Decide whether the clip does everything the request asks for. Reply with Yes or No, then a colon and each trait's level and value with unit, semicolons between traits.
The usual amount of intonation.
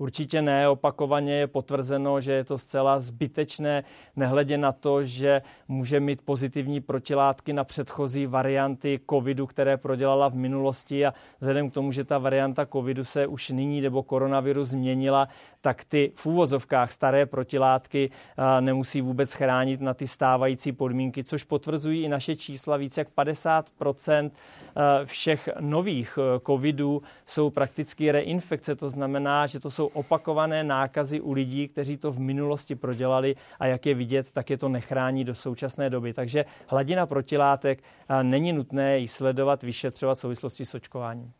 No: narrow, 1.5 semitones